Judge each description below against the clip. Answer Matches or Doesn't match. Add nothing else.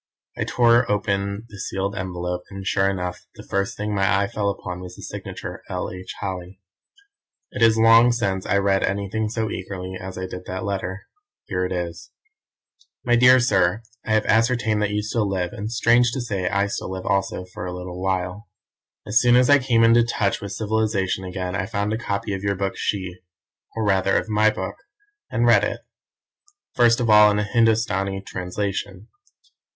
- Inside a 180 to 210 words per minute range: Matches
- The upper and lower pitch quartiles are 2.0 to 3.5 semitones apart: Matches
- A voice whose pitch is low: Matches